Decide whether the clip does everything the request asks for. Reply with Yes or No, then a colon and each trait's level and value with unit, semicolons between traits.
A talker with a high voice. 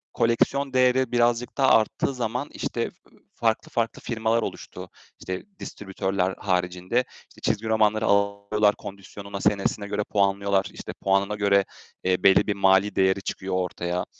No: low, 100 Hz